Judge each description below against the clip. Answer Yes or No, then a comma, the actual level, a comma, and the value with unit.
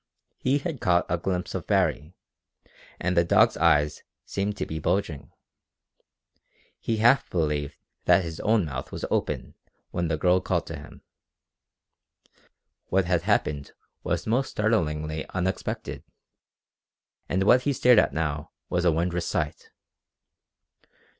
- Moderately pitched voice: No, very low, 90 Hz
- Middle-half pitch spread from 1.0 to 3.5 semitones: No, average, 5.0 semitones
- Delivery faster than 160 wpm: No, slow, 135 wpm